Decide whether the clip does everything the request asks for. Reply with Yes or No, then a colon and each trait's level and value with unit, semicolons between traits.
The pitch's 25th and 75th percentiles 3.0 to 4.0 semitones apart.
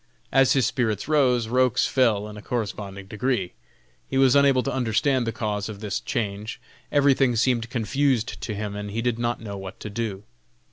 Yes: average, 3.6 semitones